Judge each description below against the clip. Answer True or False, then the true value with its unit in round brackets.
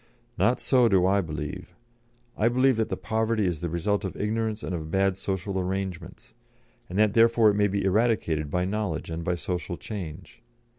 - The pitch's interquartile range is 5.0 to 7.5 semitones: False (3.7 semitones)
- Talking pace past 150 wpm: True (185 wpm)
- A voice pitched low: True (95 Hz)